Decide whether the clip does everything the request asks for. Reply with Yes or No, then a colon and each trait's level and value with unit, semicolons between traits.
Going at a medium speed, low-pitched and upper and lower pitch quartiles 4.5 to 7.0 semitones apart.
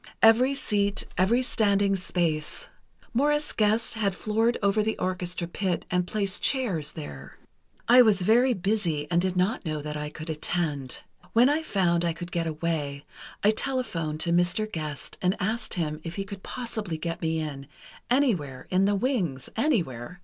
No: average, 160 wpm; medium, 185 Hz; average, 5.3 semitones